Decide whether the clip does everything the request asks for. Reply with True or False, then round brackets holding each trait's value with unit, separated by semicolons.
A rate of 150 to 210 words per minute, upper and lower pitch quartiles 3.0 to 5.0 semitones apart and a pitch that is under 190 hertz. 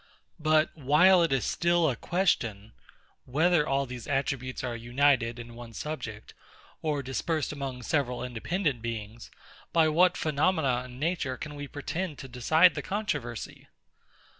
False (140 wpm; 4.6 semitones; 140 Hz)